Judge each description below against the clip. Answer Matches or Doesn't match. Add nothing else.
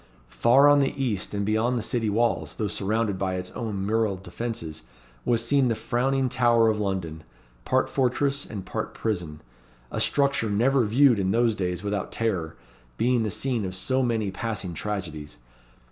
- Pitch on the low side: Matches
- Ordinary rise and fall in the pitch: Matches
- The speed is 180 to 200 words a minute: Doesn't match